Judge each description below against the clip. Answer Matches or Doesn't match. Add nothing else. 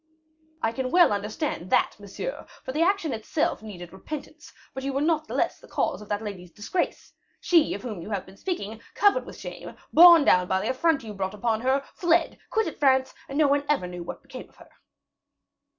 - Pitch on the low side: Doesn't match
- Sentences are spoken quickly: Matches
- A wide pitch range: Matches